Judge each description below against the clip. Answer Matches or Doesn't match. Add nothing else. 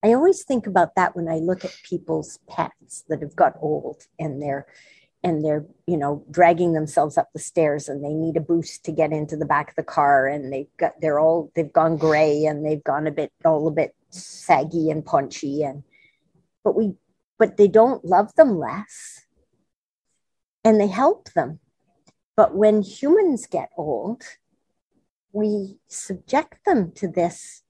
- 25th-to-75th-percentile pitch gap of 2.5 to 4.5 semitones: Doesn't match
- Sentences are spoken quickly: Doesn't match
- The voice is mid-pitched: Matches